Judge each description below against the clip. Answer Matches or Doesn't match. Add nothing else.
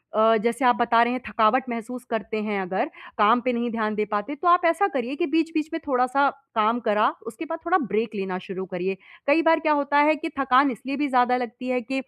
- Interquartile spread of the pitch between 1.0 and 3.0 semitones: Doesn't match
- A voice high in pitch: Matches